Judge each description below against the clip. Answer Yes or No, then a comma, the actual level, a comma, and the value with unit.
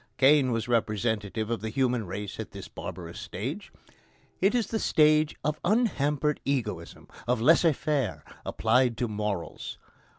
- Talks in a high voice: No, low, 125 Hz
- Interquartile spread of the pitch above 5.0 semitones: Yes, wide, 5.6 semitones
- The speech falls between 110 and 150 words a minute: Yes, average, 140 wpm